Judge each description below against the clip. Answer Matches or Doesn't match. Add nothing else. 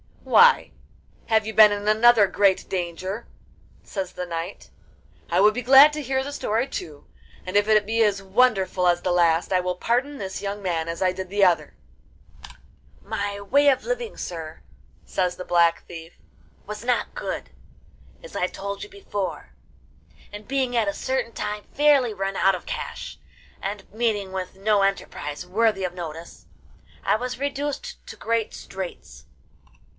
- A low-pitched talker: Doesn't match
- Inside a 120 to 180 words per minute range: Matches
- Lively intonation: Doesn't match